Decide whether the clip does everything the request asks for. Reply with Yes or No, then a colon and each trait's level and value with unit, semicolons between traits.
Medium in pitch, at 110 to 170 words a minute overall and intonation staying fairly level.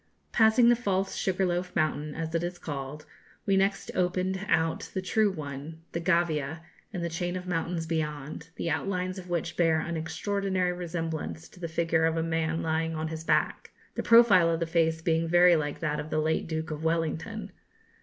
No: medium, 165 Hz; average, 190 wpm; narrow, 2.2 semitones